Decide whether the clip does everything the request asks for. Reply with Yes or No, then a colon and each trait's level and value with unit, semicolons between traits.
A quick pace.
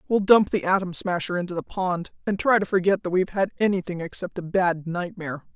Yes: fast, 215 wpm